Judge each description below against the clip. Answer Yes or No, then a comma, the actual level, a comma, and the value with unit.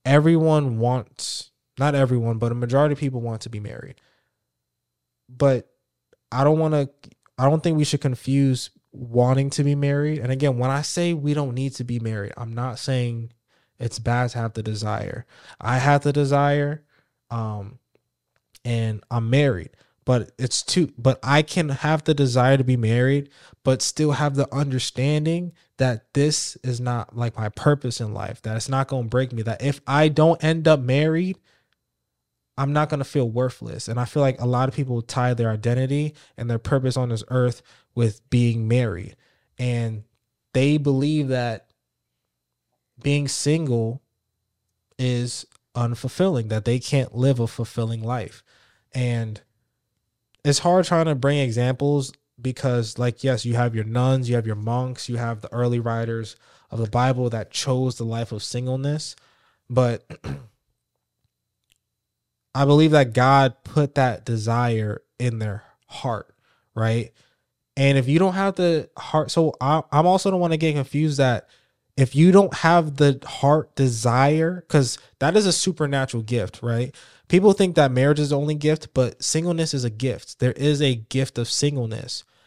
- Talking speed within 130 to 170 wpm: Yes, average, 165 wpm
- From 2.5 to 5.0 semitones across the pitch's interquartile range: Yes, average, 3.5 semitones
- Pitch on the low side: Yes, low, 130 Hz